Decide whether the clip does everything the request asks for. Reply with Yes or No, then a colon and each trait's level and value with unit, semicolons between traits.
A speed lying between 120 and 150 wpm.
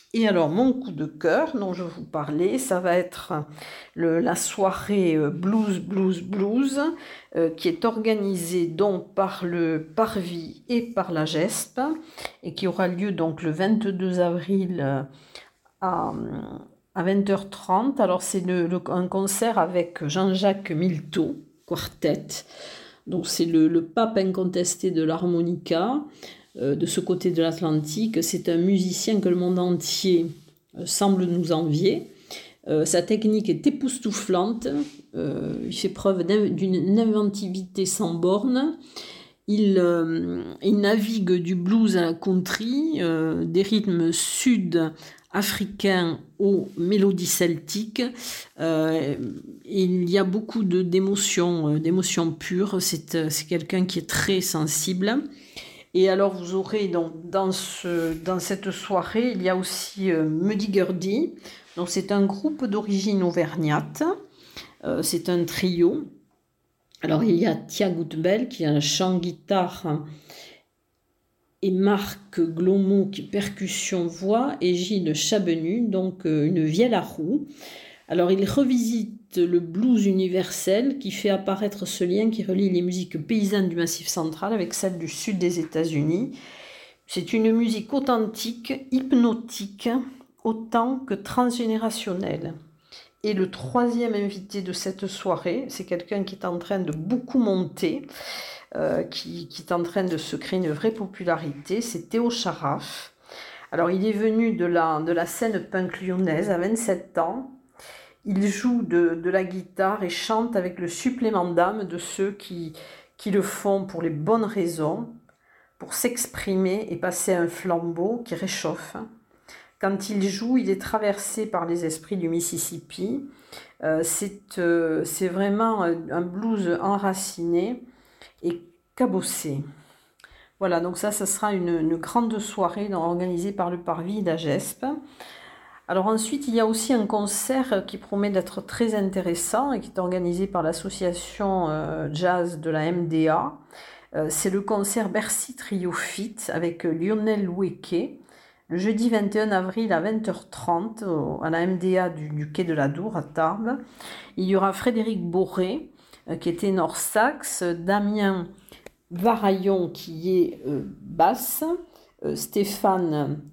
Yes: slow, 145 wpm